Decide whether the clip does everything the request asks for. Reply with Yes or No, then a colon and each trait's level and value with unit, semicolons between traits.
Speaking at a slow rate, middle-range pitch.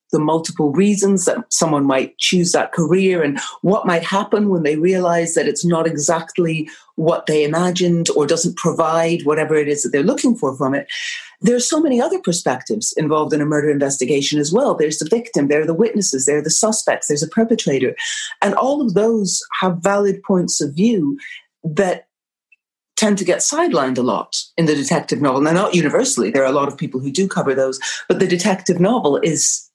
No: average, 200 wpm; medium, 175 Hz